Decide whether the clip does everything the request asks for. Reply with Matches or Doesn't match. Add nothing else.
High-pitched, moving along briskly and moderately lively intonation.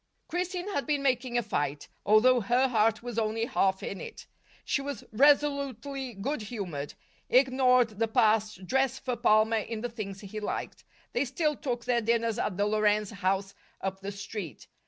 Doesn't match